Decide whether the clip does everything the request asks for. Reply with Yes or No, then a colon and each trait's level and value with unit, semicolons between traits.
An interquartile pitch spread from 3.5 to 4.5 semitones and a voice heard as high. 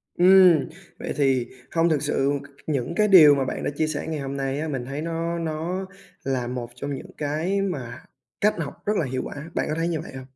No: average, 3.8 semitones; medium, 150 Hz